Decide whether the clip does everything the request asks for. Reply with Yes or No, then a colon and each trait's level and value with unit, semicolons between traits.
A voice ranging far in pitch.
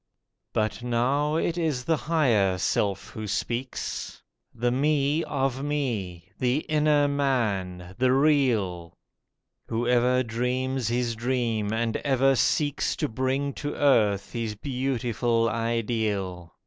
No: average, 3.9 semitones